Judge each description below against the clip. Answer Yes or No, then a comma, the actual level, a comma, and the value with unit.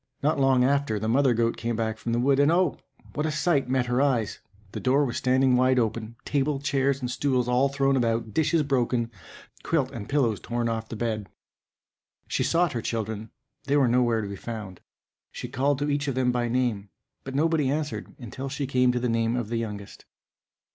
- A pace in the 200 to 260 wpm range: Yes, fast, 205 wpm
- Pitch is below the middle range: Yes, low, 125 Hz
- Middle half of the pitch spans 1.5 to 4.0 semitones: Yes, average, 3.3 semitones